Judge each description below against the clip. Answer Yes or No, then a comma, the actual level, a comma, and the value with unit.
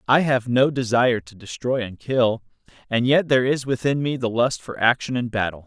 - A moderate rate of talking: No, fast, 210 wpm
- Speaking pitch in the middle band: No, low, 125 Hz